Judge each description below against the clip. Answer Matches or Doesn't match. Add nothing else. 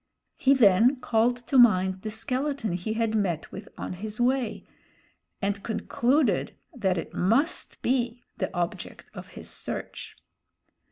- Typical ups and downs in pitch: Matches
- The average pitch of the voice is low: Doesn't match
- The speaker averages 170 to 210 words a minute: Doesn't match